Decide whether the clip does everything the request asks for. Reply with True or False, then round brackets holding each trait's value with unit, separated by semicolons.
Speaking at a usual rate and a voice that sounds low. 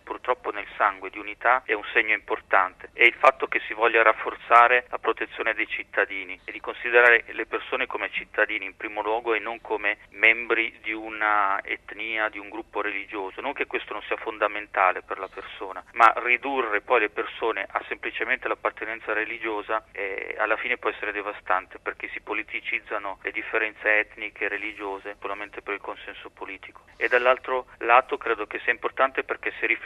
False (175 wpm; 110 Hz)